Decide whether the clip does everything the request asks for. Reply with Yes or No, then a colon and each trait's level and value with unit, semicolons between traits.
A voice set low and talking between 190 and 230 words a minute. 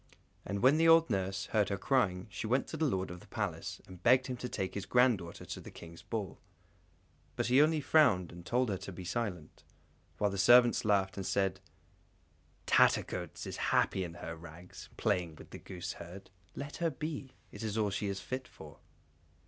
Yes: low, 100 Hz; average, 200 wpm